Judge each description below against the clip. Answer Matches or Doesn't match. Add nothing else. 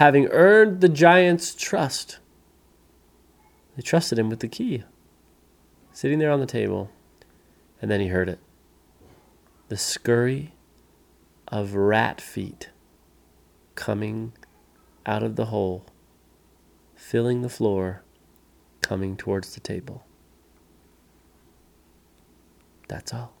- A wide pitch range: Matches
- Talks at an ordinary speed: Doesn't match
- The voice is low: Matches